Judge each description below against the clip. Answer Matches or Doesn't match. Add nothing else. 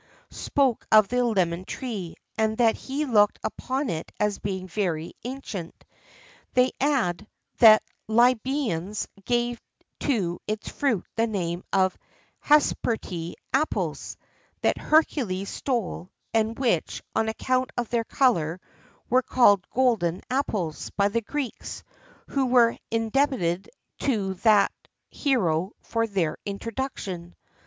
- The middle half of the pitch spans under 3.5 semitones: Doesn't match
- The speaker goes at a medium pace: Doesn't match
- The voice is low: Doesn't match